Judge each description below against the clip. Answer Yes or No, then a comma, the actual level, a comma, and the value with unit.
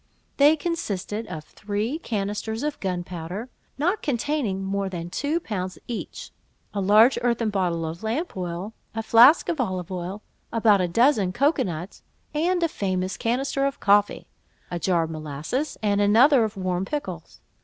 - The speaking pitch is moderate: No, high, 205 Hz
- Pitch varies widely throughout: Yes, wide, 6.1 semitones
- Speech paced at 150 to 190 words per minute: Yes, average, 155 wpm